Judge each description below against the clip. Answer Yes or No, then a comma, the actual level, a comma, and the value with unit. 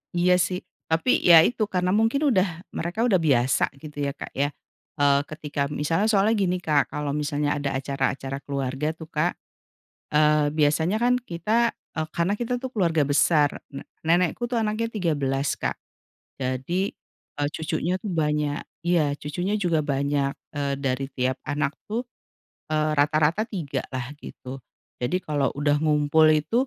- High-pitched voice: No, medium, 150 Hz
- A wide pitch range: No, average, 3.7 semitones